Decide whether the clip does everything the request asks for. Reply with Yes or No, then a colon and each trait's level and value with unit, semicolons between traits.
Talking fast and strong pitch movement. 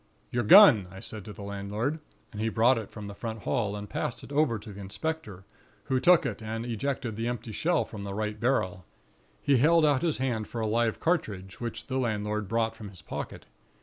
No: fast, 215 wpm; average, 4.1 semitones